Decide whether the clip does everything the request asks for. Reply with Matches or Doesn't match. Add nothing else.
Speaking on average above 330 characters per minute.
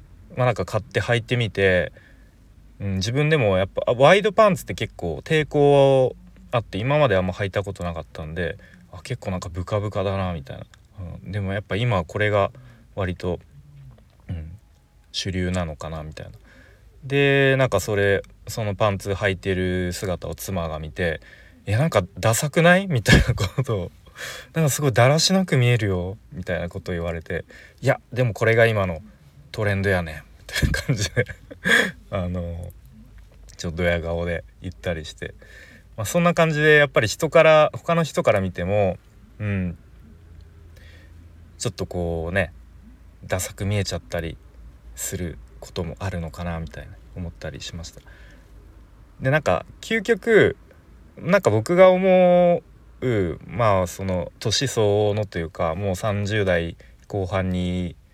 Doesn't match